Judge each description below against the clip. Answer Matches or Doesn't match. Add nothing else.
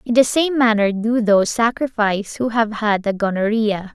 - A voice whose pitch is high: Matches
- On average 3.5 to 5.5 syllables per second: Matches